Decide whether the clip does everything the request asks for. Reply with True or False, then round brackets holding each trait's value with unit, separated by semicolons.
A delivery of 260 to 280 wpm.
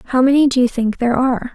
True (275 wpm)